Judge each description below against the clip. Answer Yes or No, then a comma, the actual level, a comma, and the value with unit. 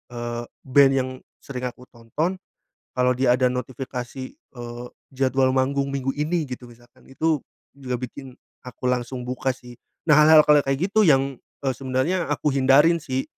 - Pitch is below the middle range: Yes, low, 130 Hz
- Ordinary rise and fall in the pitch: No, narrow, 2.0 semitones